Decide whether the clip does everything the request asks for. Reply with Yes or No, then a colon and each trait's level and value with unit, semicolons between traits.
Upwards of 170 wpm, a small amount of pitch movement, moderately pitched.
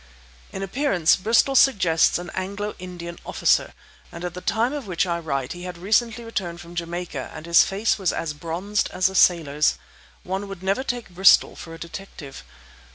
No: average, 180 wpm; average, 3.1 semitones; medium, 180 Hz